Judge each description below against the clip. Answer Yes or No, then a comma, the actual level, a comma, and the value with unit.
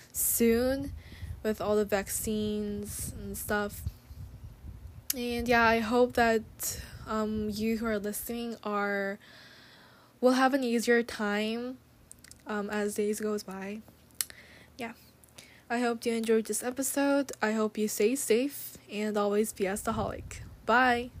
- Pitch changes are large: No, narrow, 2.2 semitones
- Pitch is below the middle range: No, high, 220 Hz